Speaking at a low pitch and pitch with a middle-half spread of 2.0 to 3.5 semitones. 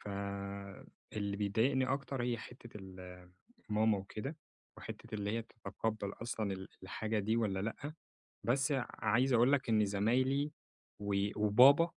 No: low, 110 Hz; average, 3.9 semitones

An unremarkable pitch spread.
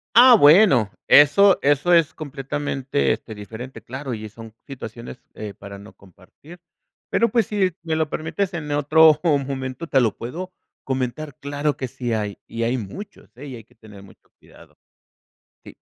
No: wide, 5.7 semitones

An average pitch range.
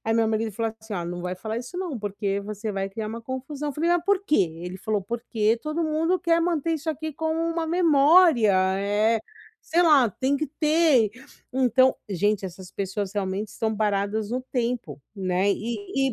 No: wide, 7.1 semitones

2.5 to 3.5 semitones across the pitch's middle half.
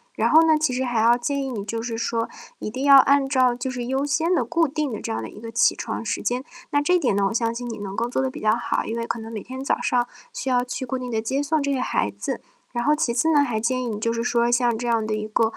Yes: average, 2.8 semitones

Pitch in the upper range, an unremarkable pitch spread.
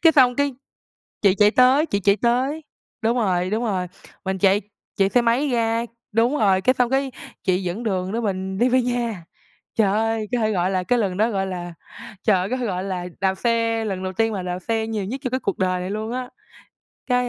Yes: high, 220 Hz; average, 4.3 semitones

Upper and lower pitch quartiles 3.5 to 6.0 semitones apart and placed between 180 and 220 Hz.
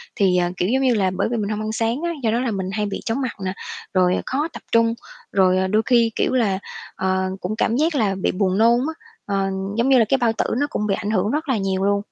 Yes: average, 4.0 semitones; high, 215 Hz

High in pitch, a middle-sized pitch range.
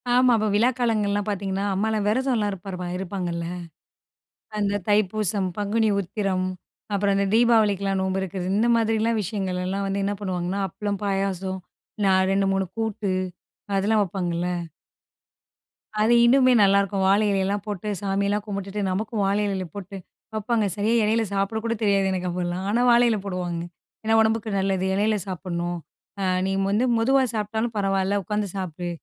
No: high, 200 Hz; narrow, 2.2 semitones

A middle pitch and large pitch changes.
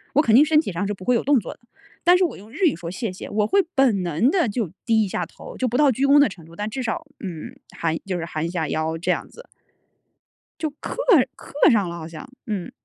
No: high, 215 Hz; wide, 7.9 semitones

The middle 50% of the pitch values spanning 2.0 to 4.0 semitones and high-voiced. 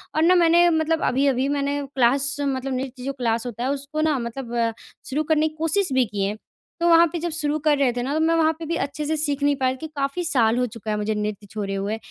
No: average, 4.4 semitones; very high, 275 Hz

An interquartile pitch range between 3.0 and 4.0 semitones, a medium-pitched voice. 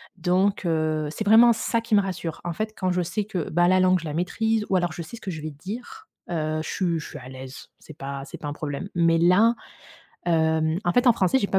No: average, 4.4 semitones; medium, 175 Hz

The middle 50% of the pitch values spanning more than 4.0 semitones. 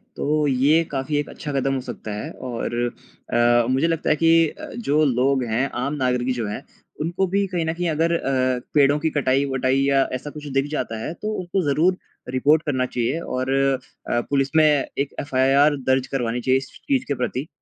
No: average, 3.2 semitones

